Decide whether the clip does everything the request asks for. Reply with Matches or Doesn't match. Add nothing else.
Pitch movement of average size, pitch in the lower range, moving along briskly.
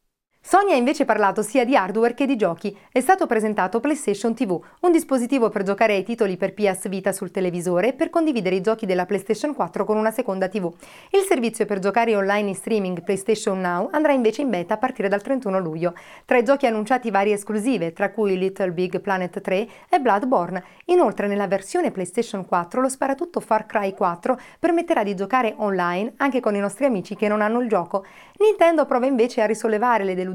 Doesn't match